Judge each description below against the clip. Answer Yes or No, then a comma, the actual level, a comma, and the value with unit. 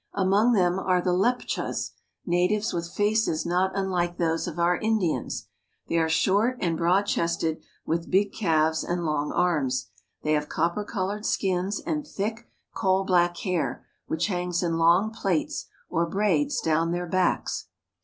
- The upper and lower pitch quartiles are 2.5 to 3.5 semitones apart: Yes, average, 2.9 semitones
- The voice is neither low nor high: Yes, medium, 180 Hz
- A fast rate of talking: No, average, 155 wpm